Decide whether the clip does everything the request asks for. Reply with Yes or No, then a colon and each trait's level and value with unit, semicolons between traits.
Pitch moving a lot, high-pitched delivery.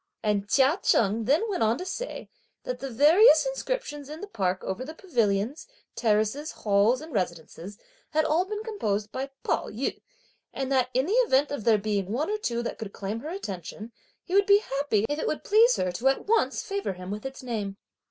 Yes: wide, 7.6 semitones; very high, 260 Hz